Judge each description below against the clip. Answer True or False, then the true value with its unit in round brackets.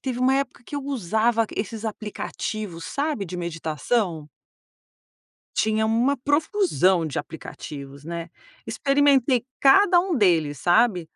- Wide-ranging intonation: True (8.0 semitones)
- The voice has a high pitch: True (220 Hz)